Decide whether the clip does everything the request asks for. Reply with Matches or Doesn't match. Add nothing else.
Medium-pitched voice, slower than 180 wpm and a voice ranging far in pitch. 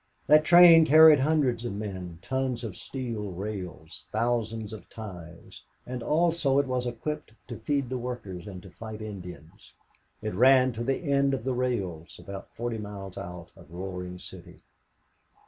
Doesn't match